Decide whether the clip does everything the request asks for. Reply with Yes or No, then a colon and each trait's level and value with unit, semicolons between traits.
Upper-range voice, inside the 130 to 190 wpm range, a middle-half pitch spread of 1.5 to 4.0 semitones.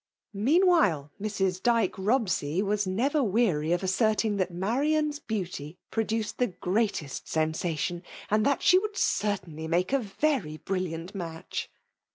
No: high, 200 Hz; average, 140 wpm; average, 5.2 semitones